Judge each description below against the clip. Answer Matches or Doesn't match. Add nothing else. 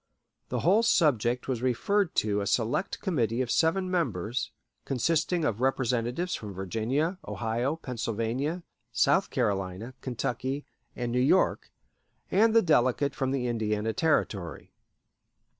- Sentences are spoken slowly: Matches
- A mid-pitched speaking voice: Doesn't match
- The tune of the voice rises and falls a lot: Matches